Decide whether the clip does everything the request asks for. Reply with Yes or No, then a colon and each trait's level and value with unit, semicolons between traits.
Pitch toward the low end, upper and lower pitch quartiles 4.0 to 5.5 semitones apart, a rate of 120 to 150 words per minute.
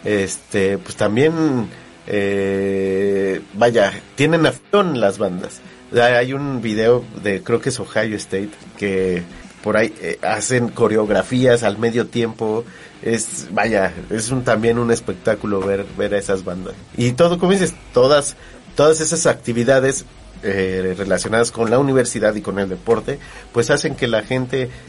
Yes: low, 115 Hz; average, 4.5 semitones; average, 145 wpm